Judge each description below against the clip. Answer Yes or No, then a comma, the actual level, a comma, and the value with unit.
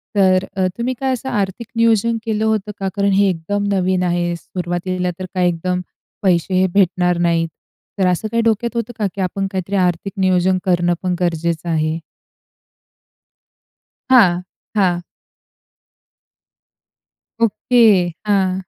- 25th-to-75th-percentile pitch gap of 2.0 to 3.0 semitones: Yes, narrow, 2.6 semitones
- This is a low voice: No, medium, 185 Hz